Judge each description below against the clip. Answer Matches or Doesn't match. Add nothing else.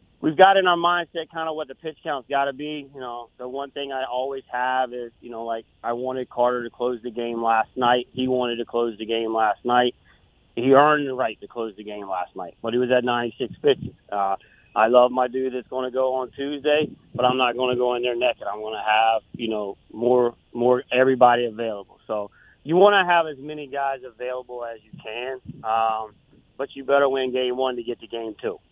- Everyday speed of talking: Doesn't match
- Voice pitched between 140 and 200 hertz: Doesn't match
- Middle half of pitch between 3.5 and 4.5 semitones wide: Doesn't match